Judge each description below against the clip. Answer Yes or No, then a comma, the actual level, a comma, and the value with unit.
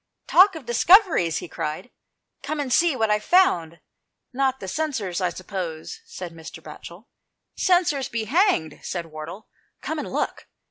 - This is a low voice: No, high, 225 Hz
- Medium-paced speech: Yes, average, 165 wpm